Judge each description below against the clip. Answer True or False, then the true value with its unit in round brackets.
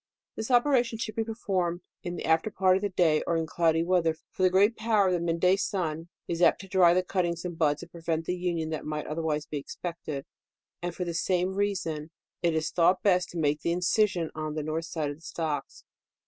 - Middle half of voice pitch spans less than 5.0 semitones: True (2.7 semitones)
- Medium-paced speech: False (235 wpm)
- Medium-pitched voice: True (175 Hz)